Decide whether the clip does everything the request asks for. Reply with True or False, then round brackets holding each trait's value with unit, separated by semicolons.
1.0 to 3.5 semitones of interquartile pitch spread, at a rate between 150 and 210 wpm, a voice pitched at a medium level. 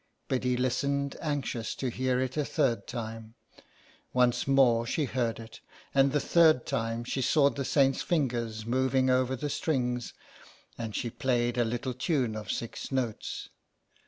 False (2.5 semitones; 155 wpm; 125 Hz)